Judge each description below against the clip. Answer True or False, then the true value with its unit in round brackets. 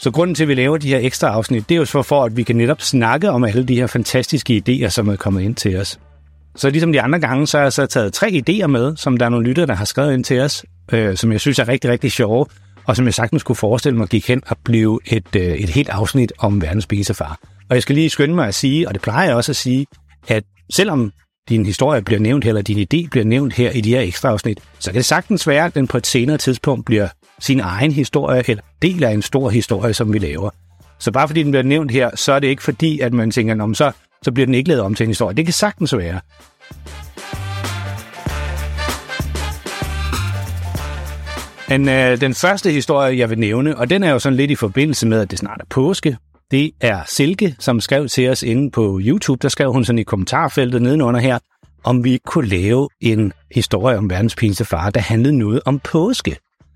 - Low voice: True (120 Hz)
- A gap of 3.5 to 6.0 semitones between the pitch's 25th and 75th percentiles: True (5.0 semitones)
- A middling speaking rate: False (235 wpm)